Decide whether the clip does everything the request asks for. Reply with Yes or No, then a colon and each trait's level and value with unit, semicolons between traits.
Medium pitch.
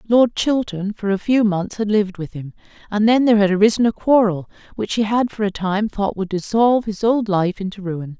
No: high, 205 Hz